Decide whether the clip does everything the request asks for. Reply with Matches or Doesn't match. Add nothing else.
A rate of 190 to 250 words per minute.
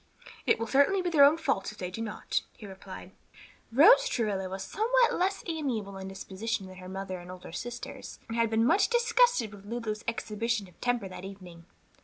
Matches